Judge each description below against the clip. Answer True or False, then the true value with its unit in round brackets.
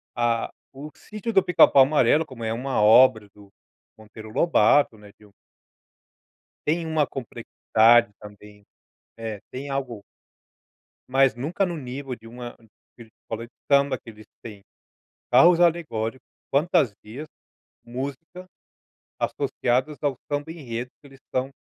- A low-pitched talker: True (130 Hz)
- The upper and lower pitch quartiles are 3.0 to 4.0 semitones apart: False (4.6 semitones)